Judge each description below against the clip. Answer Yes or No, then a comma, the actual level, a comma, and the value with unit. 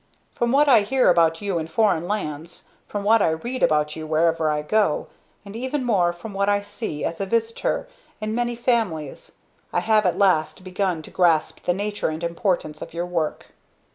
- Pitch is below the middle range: No, medium, 185 Hz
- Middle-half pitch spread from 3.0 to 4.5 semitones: No, average, 5.1 semitones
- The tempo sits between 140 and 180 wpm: No, average, 195 wpm